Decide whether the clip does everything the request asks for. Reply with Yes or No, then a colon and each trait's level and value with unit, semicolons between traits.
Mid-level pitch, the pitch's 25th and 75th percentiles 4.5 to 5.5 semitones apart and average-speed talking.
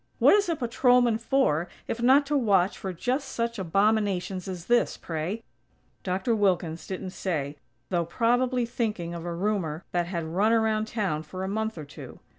No: high, 200 Hz; average, 5.1 semitones; average, 175 wpm